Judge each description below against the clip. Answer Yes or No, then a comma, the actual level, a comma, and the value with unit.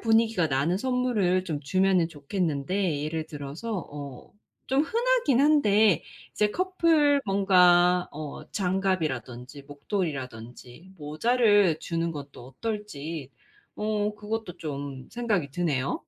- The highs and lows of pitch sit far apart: Yes, wide, 6.6 semitones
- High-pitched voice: No, medium, 180 Hz